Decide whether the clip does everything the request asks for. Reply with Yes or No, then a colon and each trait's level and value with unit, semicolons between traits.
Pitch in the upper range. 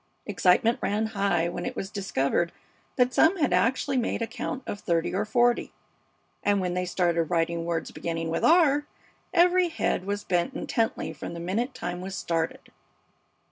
Yes: high, 195 Hz